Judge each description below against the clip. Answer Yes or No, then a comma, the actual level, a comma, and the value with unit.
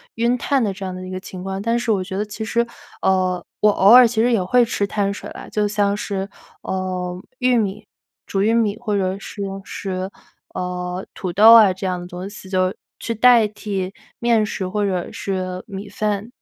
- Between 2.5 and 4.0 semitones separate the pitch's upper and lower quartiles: Yes, average, 2.8 semitones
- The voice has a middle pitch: No, high, 200 Hz